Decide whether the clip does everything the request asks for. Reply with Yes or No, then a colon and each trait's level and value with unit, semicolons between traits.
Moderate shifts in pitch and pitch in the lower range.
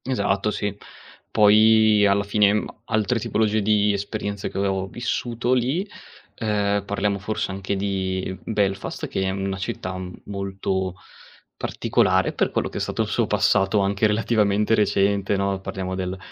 No: narrow, 1.7 semitones; low, 100 Hz